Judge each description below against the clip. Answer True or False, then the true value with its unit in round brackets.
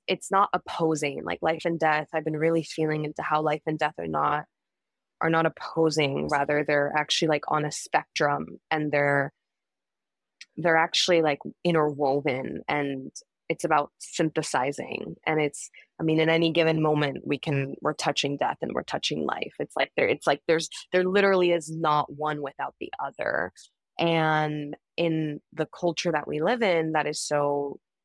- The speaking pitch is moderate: True (155 Hz)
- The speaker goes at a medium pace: True (170 wpm)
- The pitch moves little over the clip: True (1.8 semitones)